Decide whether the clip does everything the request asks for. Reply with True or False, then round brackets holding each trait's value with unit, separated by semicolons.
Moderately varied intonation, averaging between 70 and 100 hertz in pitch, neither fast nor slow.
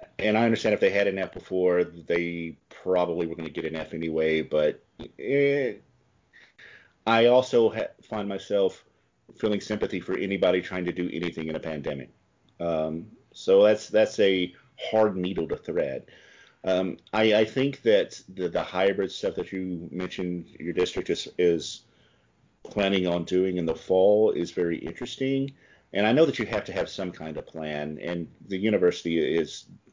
True (4.2 semitones; 90 Hz; 170 wpm)